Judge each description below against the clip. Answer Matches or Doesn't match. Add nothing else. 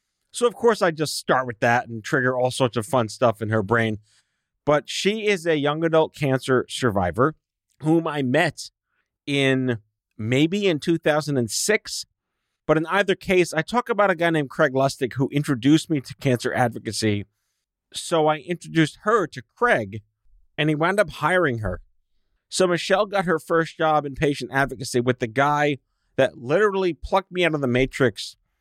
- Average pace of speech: Matches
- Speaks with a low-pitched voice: Doesn't match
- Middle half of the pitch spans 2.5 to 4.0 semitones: Doesn't match